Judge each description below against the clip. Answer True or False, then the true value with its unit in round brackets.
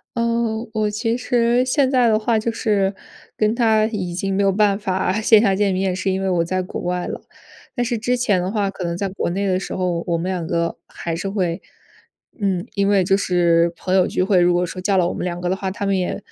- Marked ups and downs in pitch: False (3.1 semitones)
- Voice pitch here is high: True (195 Hz)